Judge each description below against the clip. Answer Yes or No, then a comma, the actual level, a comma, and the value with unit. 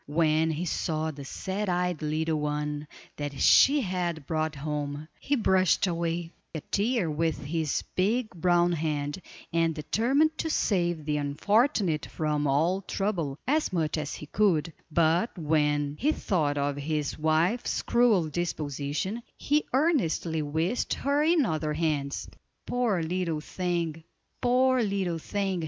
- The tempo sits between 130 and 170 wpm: Yes, average, 140 wpm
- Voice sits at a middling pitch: Yes, medium, 165 Hz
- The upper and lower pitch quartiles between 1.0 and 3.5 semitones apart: No, average, 4.6 semitones